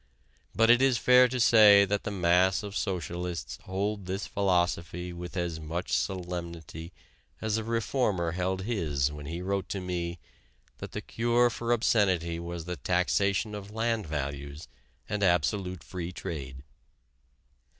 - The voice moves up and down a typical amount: Yes, average, 3.5 semitones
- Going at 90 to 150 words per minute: Yes, average, 145 wpm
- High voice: No, very low, 90 Hz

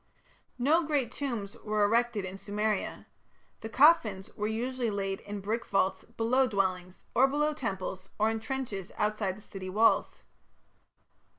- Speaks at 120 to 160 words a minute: Yes, average, 140 wpm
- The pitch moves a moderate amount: Yes, average, 4.1 semitones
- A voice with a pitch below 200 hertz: No, high, 215 Hz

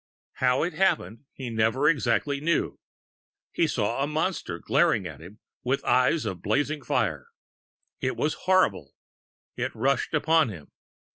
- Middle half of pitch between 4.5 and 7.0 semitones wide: Yes, wide, 5.6 semitones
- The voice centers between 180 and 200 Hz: No, low, 135 Hz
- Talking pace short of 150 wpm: Yes, average, 140 wpm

